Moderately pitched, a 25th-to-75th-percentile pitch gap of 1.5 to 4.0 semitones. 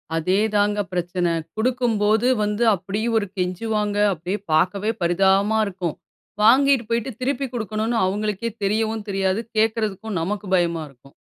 No: high, 210 Hz; average, 3.1 semitones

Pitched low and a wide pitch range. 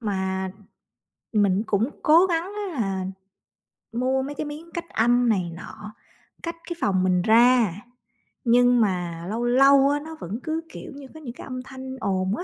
No: high, 240 Hz; wide, 6.2 semitones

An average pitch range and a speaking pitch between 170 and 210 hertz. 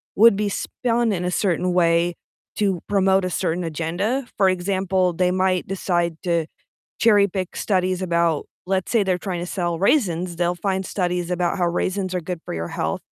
No: narrow, 2.0 semitones; medium, 185 Hz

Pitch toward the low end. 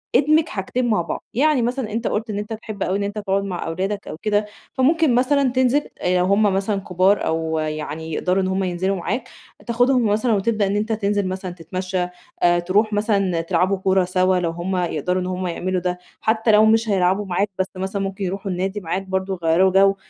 No: high, 195 Hz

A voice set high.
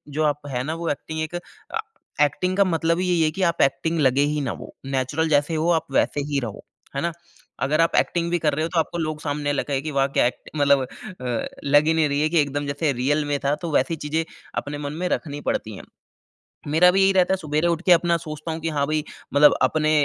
No: medium, 155 Hz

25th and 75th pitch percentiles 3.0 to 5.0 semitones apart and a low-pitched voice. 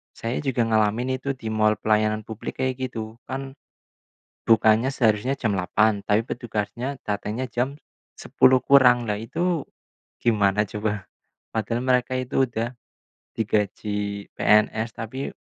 Yes: average, 3.3 semitones; low, 115 Hz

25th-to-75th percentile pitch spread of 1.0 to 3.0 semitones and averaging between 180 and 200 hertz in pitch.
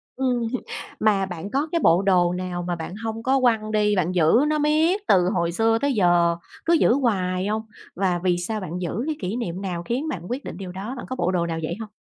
No: average, 5.2 semitones; high, 195 Hz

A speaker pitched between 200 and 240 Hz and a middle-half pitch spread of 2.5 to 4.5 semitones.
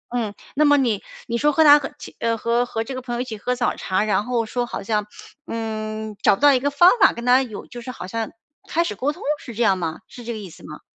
Yes: high, 235 Hz; average, 3.0 semitones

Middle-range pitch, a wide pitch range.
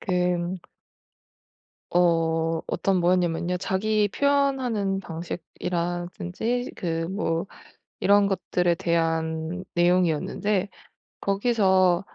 No: medium, 180 Hz; average, 2.8 semitones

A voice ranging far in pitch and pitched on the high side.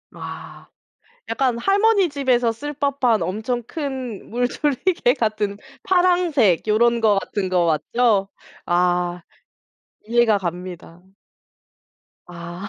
Yes: wide, 6.7 semitones; high, 230 Hz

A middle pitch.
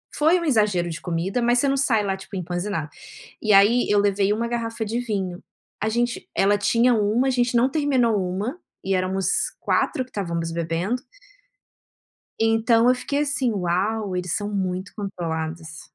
No: high, 205 Hz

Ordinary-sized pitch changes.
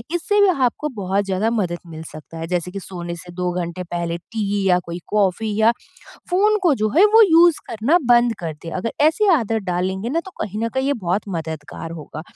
No: wide, 6.5 semitones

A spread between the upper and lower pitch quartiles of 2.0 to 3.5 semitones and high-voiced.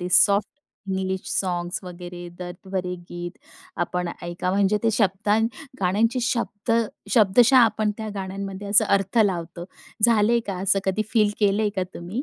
Yes: average, 2.8 semitones; high, 195 Hz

